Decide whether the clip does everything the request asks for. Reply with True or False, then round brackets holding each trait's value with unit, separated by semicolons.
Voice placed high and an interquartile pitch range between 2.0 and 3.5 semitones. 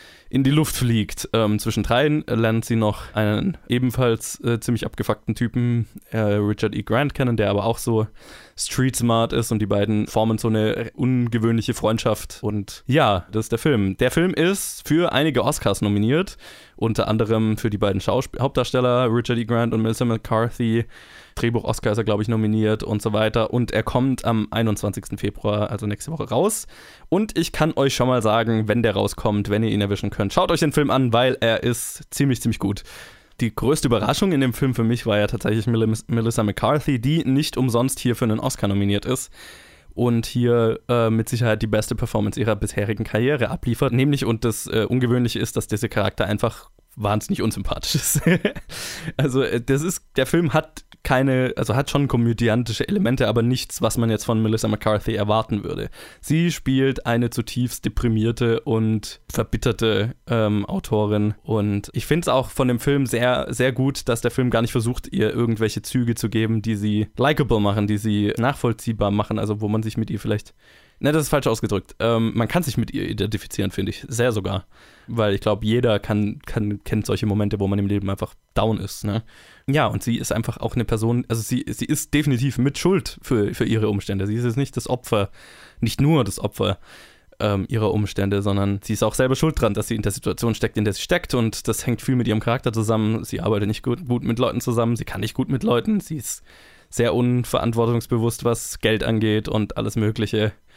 False (115 Hz; 2.8 semitones)